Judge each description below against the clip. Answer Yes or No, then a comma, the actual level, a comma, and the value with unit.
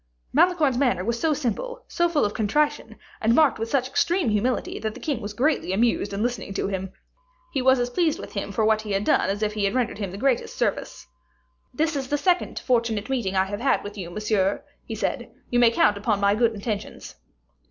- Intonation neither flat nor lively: Yes, average, 4.9 semitones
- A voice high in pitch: Yes, high, 230 Hz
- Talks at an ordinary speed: No, fast, 225 wpm